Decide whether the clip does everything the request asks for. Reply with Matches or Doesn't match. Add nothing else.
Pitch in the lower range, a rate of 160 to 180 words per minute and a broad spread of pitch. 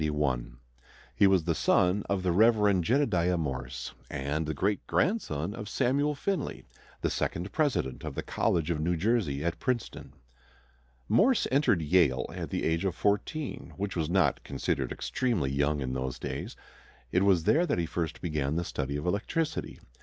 Matches